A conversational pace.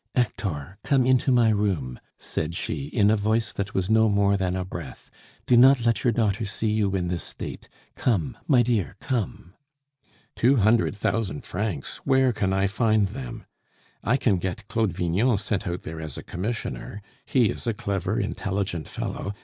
Yes: average, 175 wpm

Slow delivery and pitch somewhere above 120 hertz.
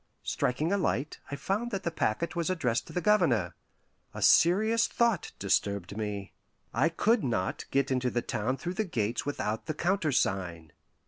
No: average, 170 wpm; medium, 140 Hz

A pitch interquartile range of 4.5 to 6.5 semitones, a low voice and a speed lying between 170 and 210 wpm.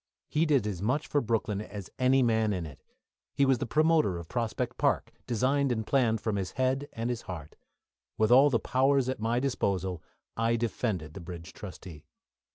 Yes: average, 4.9 semitones; low, 115 Hz; average, 180 wpm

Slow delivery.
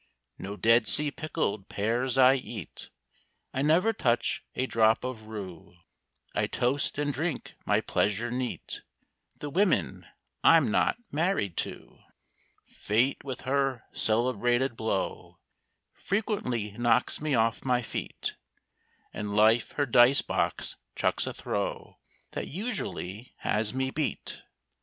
Yes: slow, 125 wpm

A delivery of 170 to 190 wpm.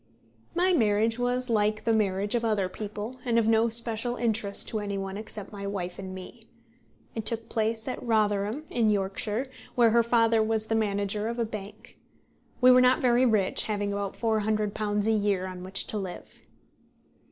Yes: average, 180 wpm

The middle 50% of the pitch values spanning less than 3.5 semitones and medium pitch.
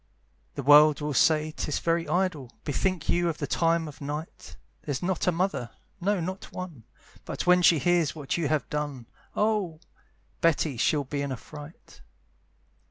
Yes: average, 3.1 semitones; medium, 155 Hz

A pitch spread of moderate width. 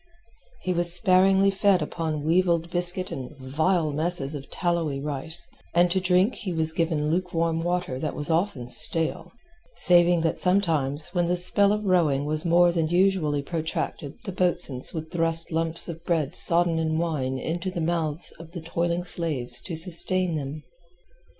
No: narrow, 2.3 semitones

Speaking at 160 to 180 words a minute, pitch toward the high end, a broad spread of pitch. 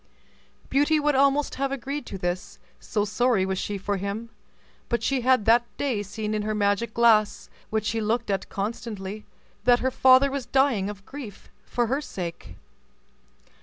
No: average, 165 wpm; high, 225 Hz; average, 4.3 semitones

